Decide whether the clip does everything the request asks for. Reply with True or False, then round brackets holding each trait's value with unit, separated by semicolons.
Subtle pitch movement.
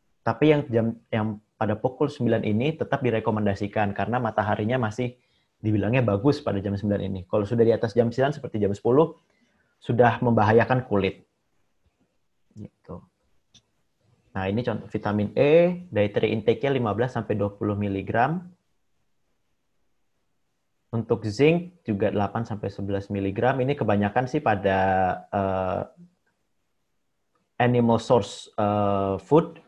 False (3.7 semitones)